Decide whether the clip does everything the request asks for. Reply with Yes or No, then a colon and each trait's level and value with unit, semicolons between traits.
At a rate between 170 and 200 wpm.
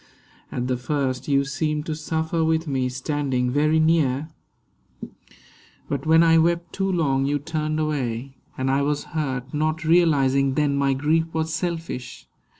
No: average, 150 wpm